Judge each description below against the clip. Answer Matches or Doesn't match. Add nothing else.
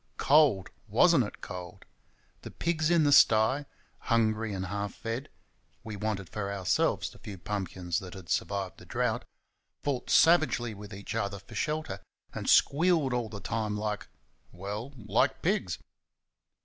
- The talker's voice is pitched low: Matches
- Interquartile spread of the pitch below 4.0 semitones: Doesn't match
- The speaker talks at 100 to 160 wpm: Matches